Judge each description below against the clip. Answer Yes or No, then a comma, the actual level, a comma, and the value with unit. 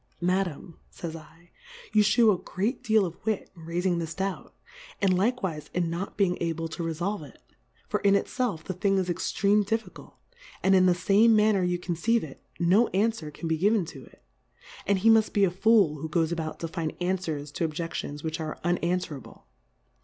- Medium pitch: Yes, medium, 180 Hz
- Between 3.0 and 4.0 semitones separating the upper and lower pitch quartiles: Yes, average, 3.6 semitones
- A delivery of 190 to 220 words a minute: Yes, average, 200 wpm